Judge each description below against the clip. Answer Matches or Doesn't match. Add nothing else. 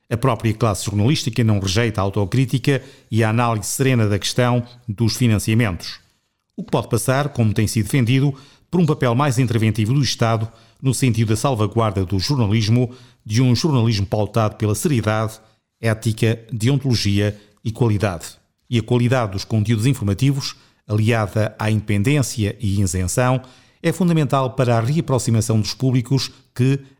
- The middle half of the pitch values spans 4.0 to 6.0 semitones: Doesn't match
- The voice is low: Matches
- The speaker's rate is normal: Matches